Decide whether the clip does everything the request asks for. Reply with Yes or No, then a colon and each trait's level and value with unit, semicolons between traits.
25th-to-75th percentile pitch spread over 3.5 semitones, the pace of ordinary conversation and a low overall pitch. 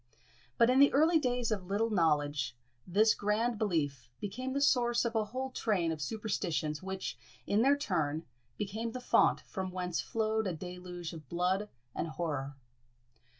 No: wide, 5.5 semitones; average, 160 wpm; high, 200 Hz